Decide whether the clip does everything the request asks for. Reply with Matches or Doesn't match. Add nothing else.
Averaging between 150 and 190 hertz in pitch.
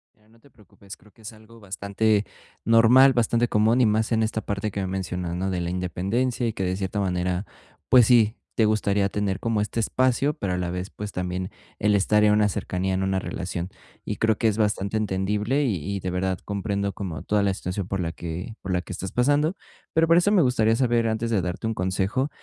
Doesn't match